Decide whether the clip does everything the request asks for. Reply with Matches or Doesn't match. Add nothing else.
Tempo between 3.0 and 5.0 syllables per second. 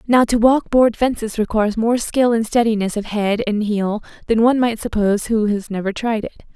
Doesn't match